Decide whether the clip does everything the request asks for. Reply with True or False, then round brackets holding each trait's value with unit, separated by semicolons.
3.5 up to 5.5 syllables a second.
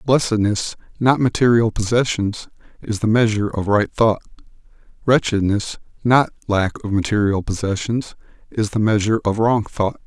True (5.0 syllables/s)